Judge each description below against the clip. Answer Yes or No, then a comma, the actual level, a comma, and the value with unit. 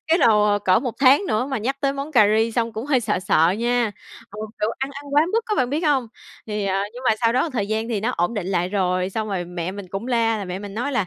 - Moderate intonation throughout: Yes, average, 4.5 semitones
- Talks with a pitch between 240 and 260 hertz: No, high, 225 Hz